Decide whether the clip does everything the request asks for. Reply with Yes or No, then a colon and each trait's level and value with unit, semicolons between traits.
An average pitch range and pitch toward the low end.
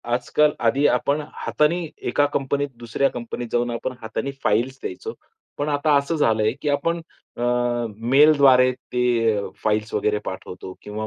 Yes: average, 4.1 semitones; low, 125 Hz